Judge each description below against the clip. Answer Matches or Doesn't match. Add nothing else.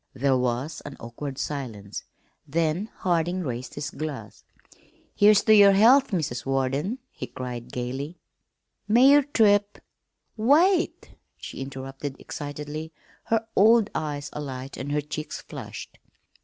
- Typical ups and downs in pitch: Doesn't match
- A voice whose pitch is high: Doesn't match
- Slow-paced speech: Matches